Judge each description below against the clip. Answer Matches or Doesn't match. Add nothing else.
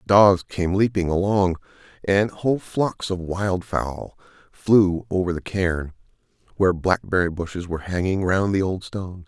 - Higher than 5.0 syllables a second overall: Doesn't match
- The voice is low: Matches